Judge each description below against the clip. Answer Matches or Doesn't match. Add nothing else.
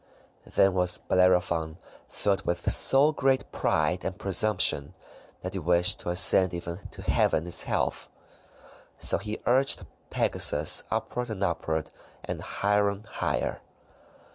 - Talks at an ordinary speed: Doesn't match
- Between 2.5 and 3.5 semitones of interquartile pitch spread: Matches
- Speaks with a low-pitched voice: Matches